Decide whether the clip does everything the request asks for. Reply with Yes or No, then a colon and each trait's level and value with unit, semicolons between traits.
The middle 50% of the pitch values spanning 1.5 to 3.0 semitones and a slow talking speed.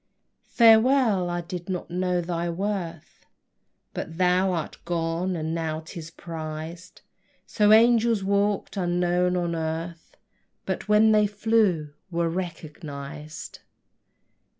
No: average, 3.4 semitones; slow, 110 wpm